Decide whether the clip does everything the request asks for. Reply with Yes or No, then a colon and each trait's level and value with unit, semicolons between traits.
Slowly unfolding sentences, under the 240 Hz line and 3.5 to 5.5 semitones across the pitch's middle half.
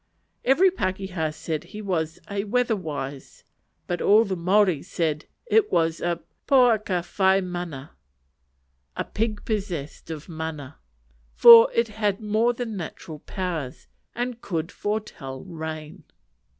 Yes: slow, 125 wpm; medium, 185 Hz; average, 5.1 semitones